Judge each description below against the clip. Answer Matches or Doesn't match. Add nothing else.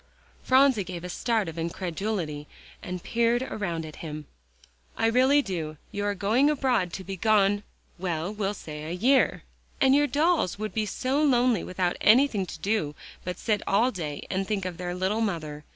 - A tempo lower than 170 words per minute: Doesn't match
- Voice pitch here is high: Matches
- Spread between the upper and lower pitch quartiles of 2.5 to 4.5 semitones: Doesn't match